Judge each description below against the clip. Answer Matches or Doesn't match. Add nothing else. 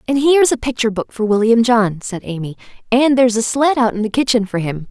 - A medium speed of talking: Doesn't match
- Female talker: Matches